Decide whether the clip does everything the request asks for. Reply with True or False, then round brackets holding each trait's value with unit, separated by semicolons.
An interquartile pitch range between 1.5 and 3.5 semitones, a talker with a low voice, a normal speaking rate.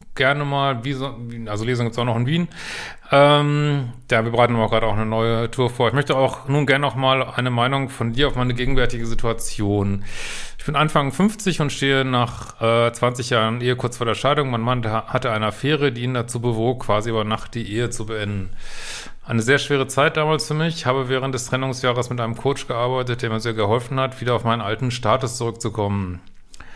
False (2.8 semitones; 125 Hz; 210 wpm)